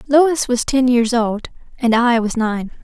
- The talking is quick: No, average, 190 wpm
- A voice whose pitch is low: No, high, 240 Hz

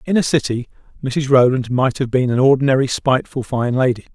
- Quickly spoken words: No, average, 190 wpm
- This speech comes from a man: Yes, male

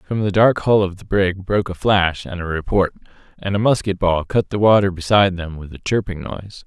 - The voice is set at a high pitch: No, very low, 95 Hz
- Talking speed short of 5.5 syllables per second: No, 5.7 syllables/s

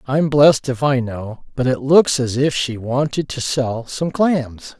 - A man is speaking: Yes, male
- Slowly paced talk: No, average, 200 wpm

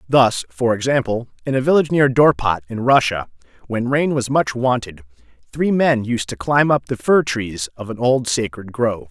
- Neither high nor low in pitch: No, low, 120 Hz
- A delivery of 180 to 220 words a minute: Yes, average, 190 wpm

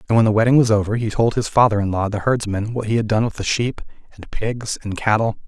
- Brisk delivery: Yes, fast, 275 wpm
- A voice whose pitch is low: Yes, low, 110 Hz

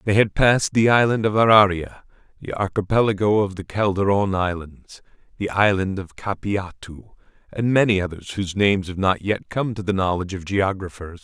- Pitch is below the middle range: Yes, low, 100 Hz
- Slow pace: No, average, 165 wpm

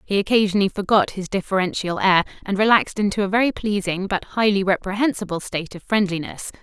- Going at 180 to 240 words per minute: No, average, 165 wpm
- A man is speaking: No, female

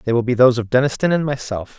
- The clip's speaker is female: No, male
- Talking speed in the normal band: No, fast, 270 wpm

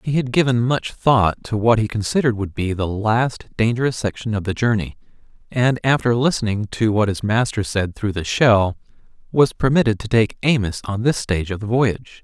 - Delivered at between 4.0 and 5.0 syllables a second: No, 5.3 syllables/s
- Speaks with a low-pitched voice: Yes, low, 110 Hz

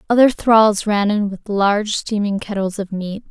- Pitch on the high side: Yes, high, 205 Hz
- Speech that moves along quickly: No, average, 180 wpm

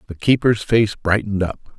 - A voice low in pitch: Yes, low, 105 Hz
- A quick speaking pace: No, average, 170 wpm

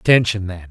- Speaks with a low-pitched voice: Yes, low, 100 Hz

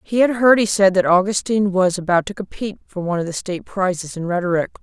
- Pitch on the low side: No, high, 190 Hz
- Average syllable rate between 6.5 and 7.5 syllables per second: Yes, 6.6 syllables/s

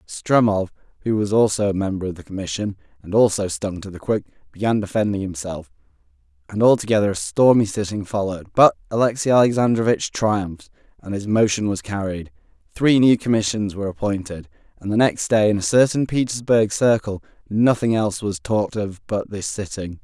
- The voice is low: Yes, low, 105 Hz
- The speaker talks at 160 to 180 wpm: Yes, average, 165 wpm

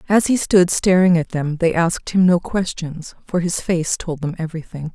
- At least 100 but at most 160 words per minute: No, fast, 205 wpm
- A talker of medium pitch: Yes, medium, 170 Hz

